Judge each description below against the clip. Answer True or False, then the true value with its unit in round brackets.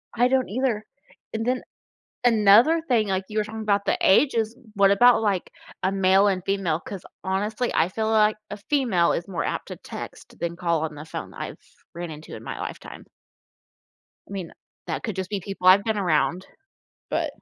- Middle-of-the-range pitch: False (200 Hz)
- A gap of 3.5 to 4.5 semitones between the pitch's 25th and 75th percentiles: False (3.1 semitones)